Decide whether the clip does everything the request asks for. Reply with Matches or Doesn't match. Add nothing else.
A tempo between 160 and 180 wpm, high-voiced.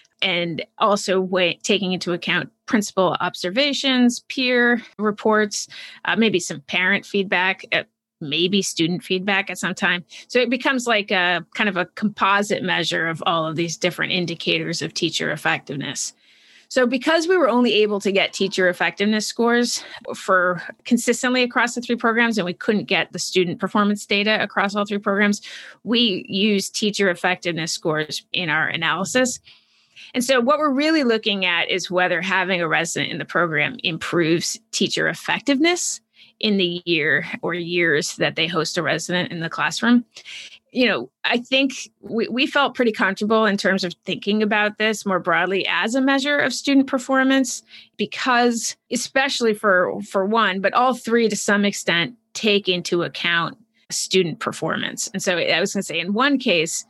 Matches